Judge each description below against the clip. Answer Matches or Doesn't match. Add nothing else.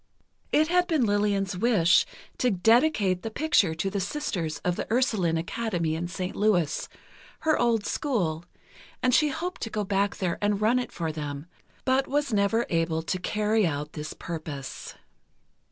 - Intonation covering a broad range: Matches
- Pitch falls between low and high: Doesn't match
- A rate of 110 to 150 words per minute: Doesn't match